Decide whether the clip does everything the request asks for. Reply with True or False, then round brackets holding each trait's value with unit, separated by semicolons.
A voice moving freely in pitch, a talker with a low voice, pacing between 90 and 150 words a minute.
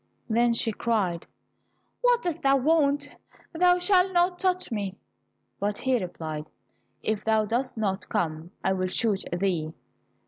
False (8.9 semitones; 225 Hz; 140 wpm)